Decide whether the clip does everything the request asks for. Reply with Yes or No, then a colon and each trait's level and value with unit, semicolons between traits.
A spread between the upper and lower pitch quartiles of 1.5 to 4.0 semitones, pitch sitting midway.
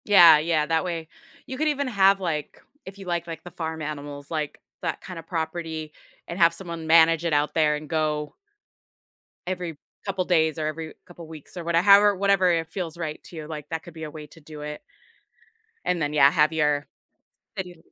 Yes: narrow, 2.6 semitones; medium, 165 Hz